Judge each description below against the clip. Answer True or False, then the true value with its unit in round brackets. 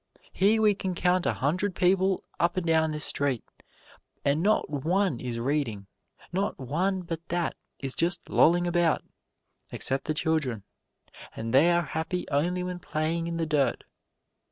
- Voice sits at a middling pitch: True (165 Hz)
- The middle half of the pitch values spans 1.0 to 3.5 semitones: False (4.0 semitones)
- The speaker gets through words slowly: False (155 wpm)